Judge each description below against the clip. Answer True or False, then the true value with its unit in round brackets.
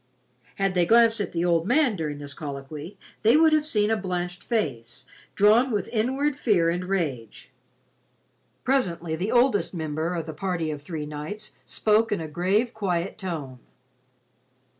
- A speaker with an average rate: True (160 wpm)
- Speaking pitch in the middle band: True (180 Hz)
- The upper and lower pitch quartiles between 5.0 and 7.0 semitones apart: True (5.6 semitones)